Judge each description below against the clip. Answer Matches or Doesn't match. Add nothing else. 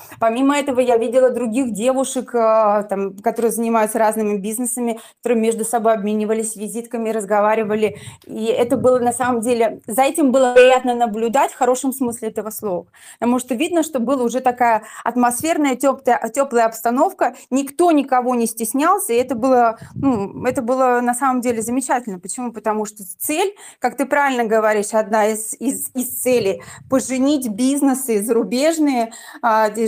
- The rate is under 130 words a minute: Doesn't match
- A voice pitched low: Doesn't match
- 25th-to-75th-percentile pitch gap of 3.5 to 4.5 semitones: Doesn't match